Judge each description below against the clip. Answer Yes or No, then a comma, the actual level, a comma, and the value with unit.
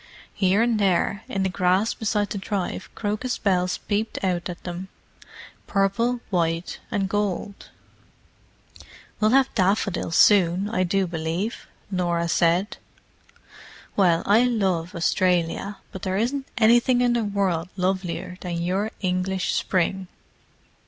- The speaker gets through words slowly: Yes, slow, 125 wpm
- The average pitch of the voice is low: No, high, 190 Hz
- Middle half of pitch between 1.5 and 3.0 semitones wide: Yes, average, 2.7 semitones